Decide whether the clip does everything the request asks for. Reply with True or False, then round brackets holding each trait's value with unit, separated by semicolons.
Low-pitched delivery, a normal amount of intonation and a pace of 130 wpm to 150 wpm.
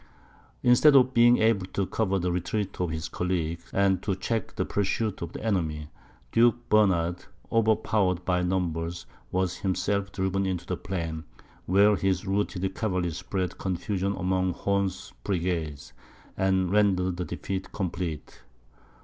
False (95 Hz; 2.2 semitones; 140 wpm)